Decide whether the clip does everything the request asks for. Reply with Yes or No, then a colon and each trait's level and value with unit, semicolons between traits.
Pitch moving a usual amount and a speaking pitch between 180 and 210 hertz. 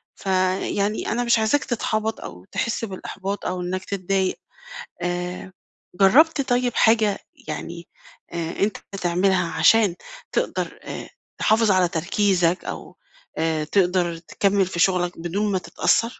Yes: average, 3.3 semitones; high, 190 Hz